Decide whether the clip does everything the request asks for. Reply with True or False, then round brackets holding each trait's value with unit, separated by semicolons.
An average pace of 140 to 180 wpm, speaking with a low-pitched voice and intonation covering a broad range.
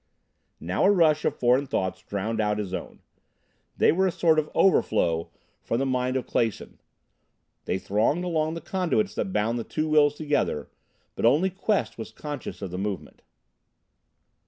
True (165 wpm; 130 Hz; 7.3 semitones)